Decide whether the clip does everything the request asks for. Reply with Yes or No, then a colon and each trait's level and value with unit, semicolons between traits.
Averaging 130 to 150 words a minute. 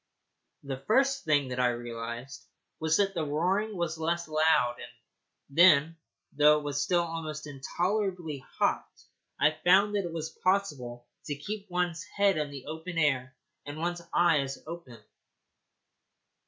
Yes: average, 145 wpm